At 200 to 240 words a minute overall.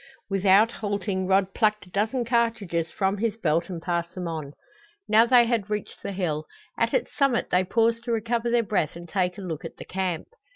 Yes: fast, 205 wpm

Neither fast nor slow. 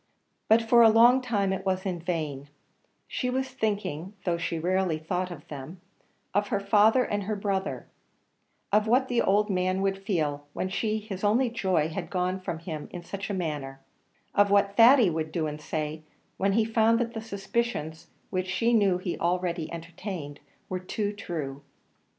Yes: average, 180 wpm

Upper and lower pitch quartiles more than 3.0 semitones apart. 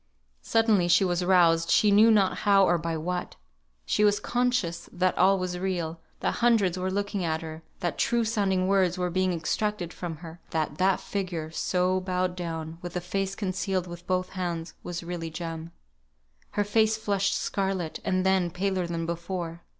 No: narrow, 2.4 semitones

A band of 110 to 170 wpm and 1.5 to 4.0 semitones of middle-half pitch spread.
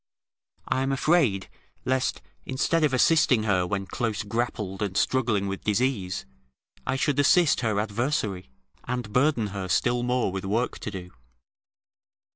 No: average, 140 wpm; average, 4.8 semitones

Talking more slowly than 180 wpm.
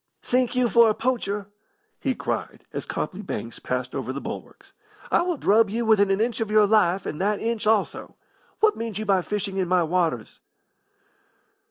No: average, 185 wpm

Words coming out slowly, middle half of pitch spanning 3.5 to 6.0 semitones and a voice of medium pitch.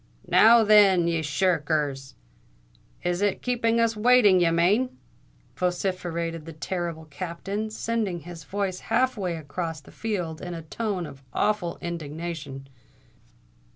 Yes: slow, 130 wpm; average, 4.4 semitones; medium, 175 Hz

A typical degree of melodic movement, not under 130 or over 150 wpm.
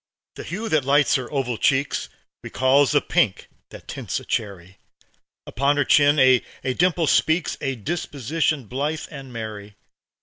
Yes: average, 3.3 semitones; average, 145 wpm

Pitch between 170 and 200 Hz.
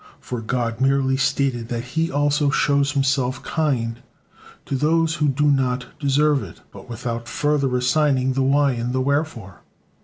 No: low, 135 Hz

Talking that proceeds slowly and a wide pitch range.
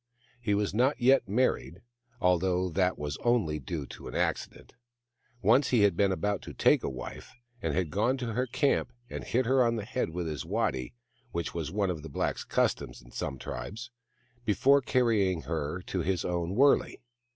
No: average, 185 wpm; wide, 6.3 semitones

